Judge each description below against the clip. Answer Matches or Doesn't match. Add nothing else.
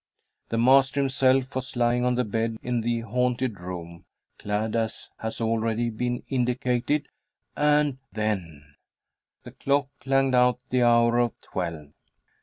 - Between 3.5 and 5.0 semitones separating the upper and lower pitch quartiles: Doesn't match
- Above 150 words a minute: Doesn't match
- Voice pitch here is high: Doesn't match